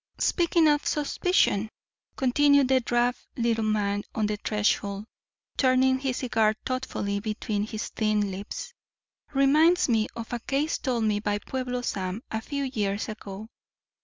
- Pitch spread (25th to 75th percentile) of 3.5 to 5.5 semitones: Yes, average, 4.1 semitones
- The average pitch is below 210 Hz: No, high, 230 Hz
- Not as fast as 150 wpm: Yes, average, 140 wpm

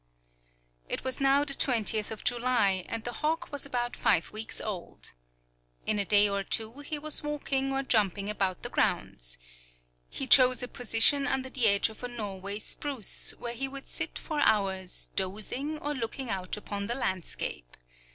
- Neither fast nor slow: Yes, average, 170 wpm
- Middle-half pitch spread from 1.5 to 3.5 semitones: No, average, 5.2 semitones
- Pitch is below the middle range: No, high, 235 Hz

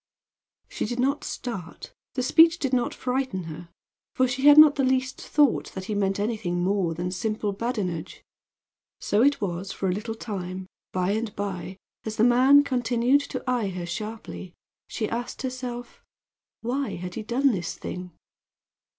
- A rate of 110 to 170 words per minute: Yes, average, 165 wpm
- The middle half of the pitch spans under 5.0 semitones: No, average, 5.3 semitones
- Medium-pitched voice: No, high, 225 Hz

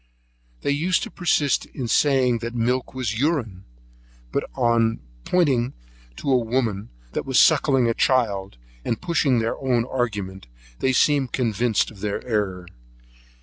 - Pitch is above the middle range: No, low, 120 Hz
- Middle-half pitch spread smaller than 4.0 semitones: Yes, average, 3.2 semitones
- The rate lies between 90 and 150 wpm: Yes, average, 145 wpm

